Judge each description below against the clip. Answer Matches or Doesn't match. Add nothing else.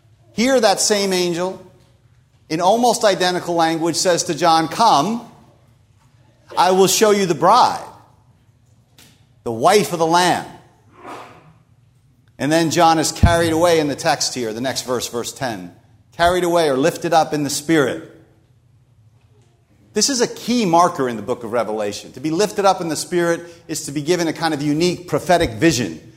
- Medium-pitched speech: Matches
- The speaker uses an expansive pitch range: Matches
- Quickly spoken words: Doesn't match